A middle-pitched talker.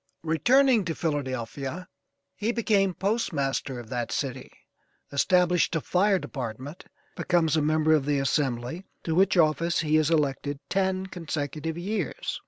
Yes: medium, 160 Hz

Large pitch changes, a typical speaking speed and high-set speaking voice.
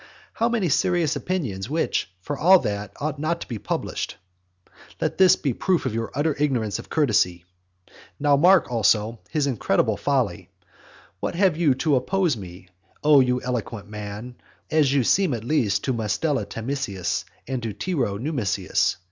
No: wide, 6.4 semitones; average, 165 wpm; low, 130 Hz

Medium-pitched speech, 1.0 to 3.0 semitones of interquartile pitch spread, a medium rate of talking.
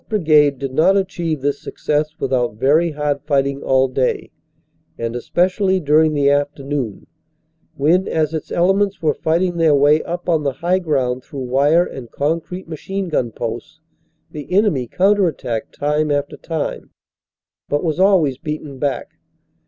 No: medium, 150 Hz; average, 3.8 semitones; average, 150 wpm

